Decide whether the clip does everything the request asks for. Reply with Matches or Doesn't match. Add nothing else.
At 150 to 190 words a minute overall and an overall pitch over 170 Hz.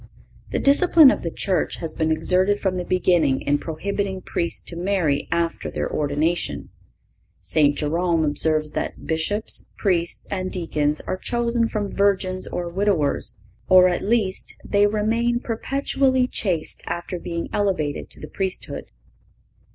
Doesn't match